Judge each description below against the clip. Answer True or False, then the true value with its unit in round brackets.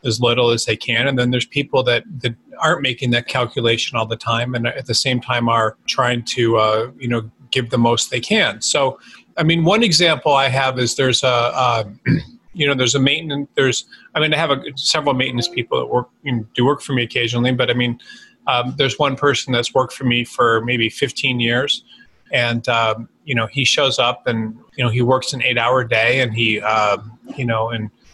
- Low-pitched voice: True (125 Hz)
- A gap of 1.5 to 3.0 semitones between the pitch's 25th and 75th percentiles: True (2.6 semitones)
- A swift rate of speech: True (225 wpm)